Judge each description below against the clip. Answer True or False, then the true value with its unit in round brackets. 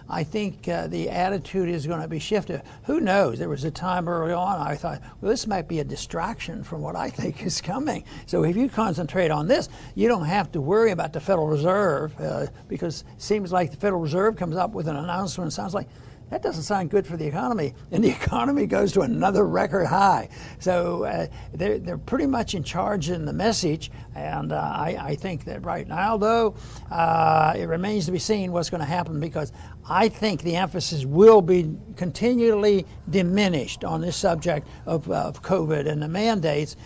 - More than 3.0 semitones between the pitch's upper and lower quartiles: True (4.2 semitones)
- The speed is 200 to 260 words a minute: True (205 wpm)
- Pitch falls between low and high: True (175 Hz)